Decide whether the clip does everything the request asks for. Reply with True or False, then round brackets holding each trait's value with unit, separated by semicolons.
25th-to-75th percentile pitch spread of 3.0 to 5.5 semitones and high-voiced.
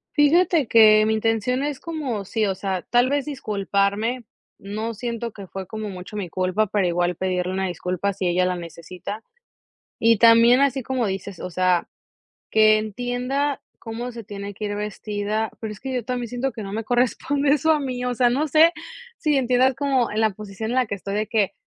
True (4.1 semitones; 220 Hz)